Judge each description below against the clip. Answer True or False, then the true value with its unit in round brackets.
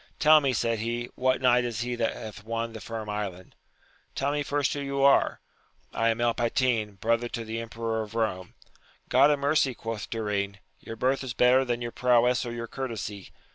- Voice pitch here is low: True (115 Hz)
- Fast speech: True (215 wpm)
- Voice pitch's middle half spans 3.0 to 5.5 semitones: False (2.4 semitones)